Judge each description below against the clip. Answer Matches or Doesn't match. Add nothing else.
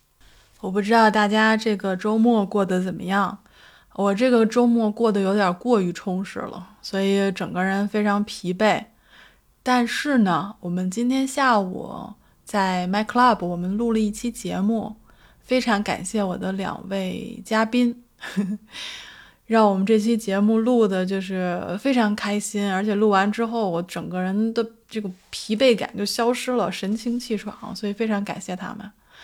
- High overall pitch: Matches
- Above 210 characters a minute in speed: Matches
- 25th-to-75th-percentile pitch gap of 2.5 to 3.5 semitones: Matches